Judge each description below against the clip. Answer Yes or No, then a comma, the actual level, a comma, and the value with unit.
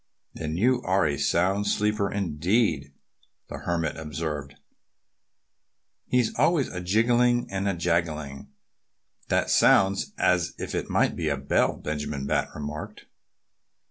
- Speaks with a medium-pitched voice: No, very low, 85 Hz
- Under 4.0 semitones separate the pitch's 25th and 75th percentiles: No, average, 5.2 semitones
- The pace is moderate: No, slow, 125 wpm